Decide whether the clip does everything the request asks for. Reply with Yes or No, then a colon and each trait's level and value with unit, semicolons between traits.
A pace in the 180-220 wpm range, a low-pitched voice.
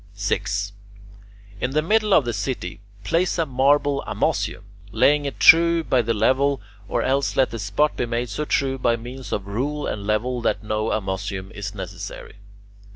No: average, 170 wpm; low, 125 Hz